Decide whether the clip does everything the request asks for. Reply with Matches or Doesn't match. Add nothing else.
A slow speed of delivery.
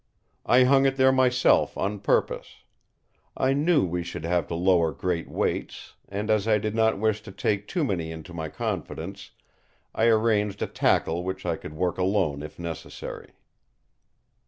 Doesn't match